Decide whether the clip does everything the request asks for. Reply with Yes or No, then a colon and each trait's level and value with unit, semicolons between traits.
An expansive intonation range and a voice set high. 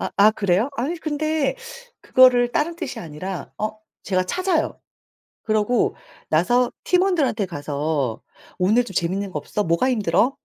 Yes: wide, 7.3 semitones; high, 215 Hz